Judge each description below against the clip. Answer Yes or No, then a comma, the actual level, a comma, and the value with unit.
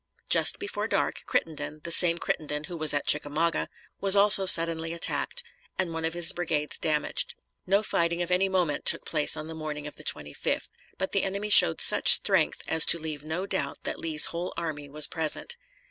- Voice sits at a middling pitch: Yes, medium, 165 Hz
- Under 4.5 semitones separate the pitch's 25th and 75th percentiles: Yes, average, 2.9 semitones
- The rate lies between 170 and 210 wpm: Yes, average, 190 wpm